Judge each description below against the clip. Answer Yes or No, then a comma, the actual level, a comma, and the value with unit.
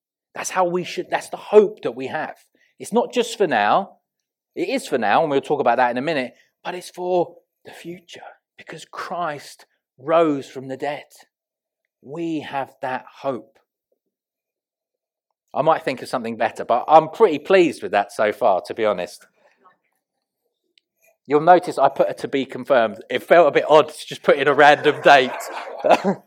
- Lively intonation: Yes, wide, 6.5 semitones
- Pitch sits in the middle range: Yes, medium, 175 Hz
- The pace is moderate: Yes, average, 180 wpm